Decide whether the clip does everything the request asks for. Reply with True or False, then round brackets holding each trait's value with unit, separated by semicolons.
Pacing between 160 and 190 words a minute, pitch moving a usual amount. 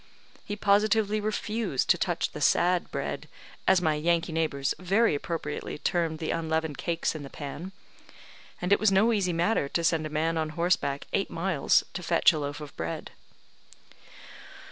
True (165 wpm; 3.7 semitones)